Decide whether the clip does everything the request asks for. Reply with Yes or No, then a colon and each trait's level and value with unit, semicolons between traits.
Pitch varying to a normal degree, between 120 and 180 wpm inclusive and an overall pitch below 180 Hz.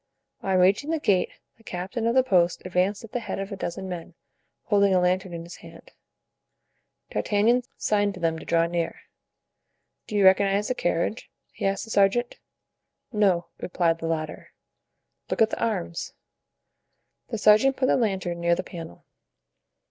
No: average, 3.6 semitones; average, 165 wpm; high, 195 Hz